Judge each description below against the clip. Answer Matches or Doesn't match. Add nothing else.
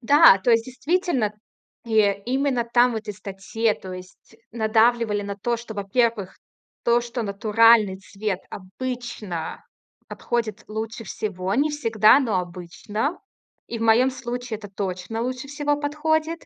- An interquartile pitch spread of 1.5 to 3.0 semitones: Doesn't match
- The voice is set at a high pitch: Matches